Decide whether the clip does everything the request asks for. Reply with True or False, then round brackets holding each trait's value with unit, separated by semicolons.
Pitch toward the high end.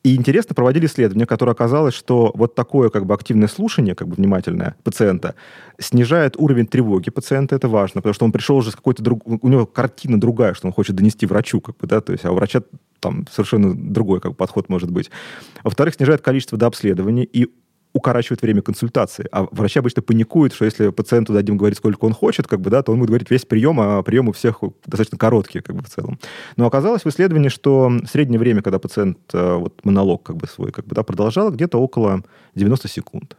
False (120 Hz)